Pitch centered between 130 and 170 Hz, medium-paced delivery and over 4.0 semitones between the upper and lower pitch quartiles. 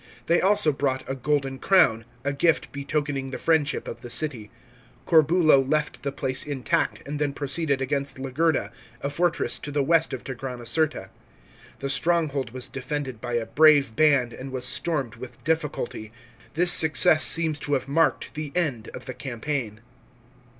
No: medium, 140 Hz; average, 160 wpm; average, 3.1 semitones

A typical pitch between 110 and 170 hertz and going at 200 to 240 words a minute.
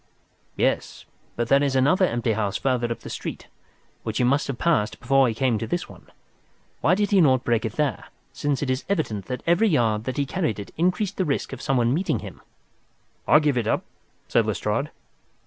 Yes: low, 135 Hz; fast, 205 wpm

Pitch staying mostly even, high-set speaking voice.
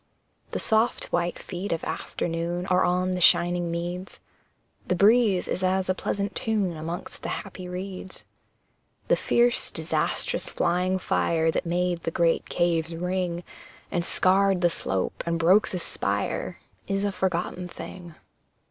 No: narrow, 1.7 semitones; medium, 180 Hz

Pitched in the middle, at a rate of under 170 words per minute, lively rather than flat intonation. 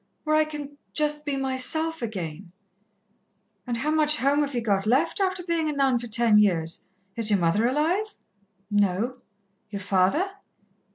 No: very high, 255 Hz; average, 160 wpm; wide, 6.6 semitones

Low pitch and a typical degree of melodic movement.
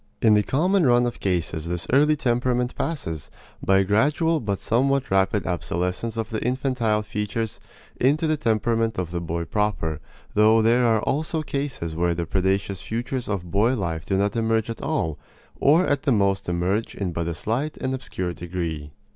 No: low, 110 Hz; wide, 5.7 semitones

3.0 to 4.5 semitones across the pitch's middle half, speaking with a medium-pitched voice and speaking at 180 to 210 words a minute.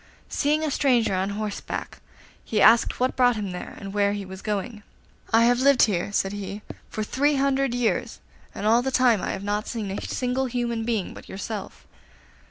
No: average, 3.6 semitones; high, 225 Hz; average, 190 wpm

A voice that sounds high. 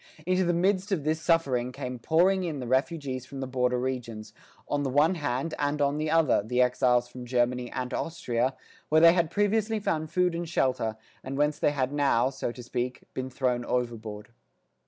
No: low, 135 Hz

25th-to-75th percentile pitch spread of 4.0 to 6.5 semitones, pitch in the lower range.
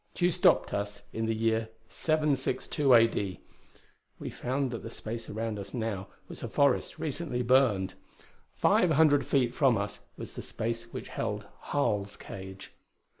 Yes: average, 5.0 semitones; low, 115 Hz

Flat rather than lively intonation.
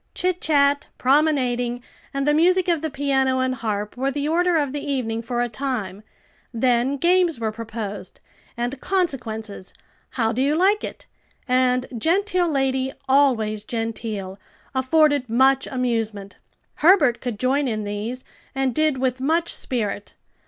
No: average, 4.2 semitones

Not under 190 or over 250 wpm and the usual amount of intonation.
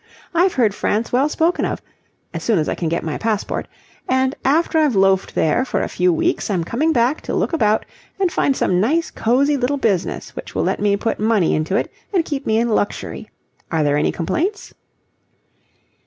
No: average, 200 wpm; wide, 6.9 semitones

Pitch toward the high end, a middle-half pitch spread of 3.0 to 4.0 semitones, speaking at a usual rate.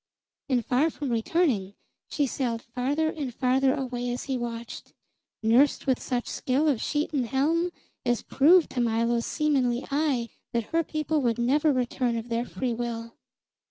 Yes: very high, 255 Hz; average, 3.5 semitones; average, 160 wpm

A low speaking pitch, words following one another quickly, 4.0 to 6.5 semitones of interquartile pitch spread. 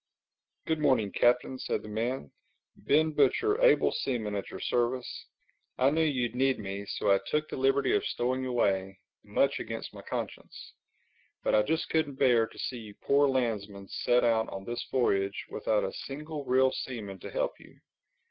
No: low, 125 Hz; average, 170 wpm; average, 4.6 semitones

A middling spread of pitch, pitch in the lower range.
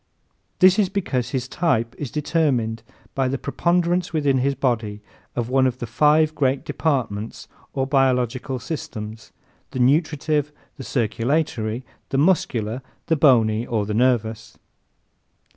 Yes: average, 4.5 semitones; low, 130 Hz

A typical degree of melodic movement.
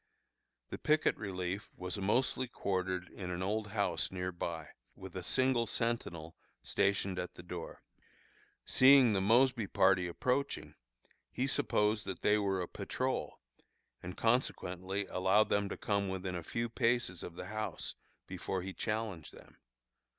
Yes: average, 3.7 semitones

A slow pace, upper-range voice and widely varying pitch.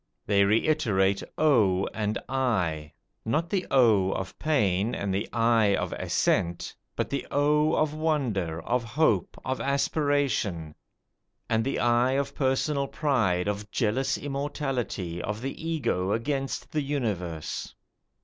No: slow, 130 wpm; low, 120 Hz; wide, 6.1 semitones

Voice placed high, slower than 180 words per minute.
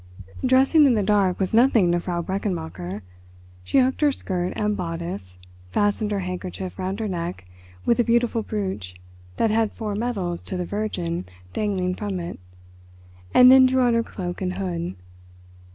Yes: high, 195 Hz; average, 165 wpm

